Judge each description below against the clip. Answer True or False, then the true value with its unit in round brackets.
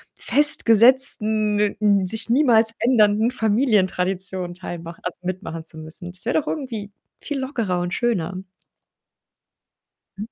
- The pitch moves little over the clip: False (4.4 semitones)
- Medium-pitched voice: False (210 Hz)